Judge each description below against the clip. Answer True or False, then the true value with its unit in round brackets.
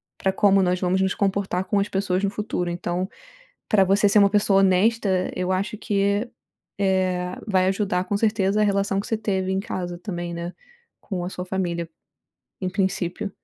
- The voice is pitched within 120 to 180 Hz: False (190 Hz)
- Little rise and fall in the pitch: True (1.8 semitones)